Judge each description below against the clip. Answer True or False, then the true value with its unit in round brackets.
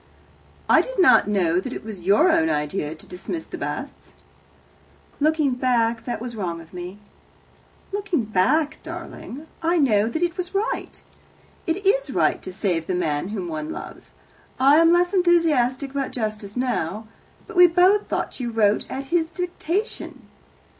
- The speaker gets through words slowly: False (160 wpm)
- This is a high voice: True (255 Hz)